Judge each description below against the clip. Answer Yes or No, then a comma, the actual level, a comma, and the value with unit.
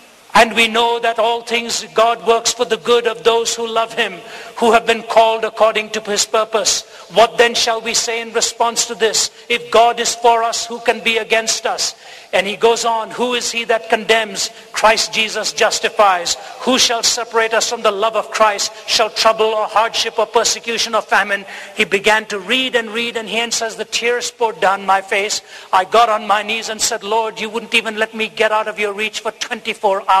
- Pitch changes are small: Yes, narrow, 1.2 semitones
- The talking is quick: Yes, fast, 215 wpm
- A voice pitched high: Yes, high, 225 Hz